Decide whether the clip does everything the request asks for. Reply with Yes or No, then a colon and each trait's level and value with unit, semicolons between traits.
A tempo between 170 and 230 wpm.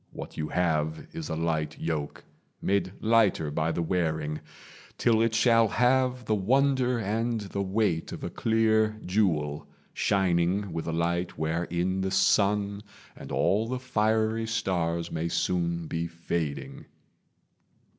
No: slow, 135 wpm